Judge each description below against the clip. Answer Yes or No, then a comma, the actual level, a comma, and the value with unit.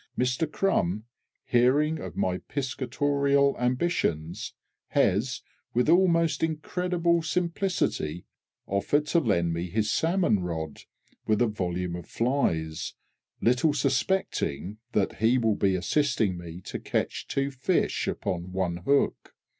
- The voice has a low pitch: Yes, low, 125 Hz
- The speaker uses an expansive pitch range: Yes, wide, 8.7 semitones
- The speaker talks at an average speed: No, slow, 120 wpm